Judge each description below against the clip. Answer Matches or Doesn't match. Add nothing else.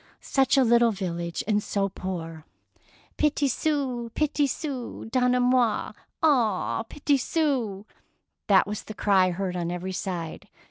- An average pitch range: Doesn't match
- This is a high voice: Matches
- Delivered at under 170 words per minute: Matches